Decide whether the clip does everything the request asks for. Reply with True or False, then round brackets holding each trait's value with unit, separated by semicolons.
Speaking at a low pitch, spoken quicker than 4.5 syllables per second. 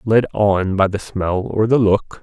False (105 Hz; 3.8 syllables/s)